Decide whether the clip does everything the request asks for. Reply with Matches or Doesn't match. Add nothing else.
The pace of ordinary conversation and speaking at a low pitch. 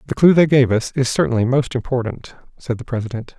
Doesn't match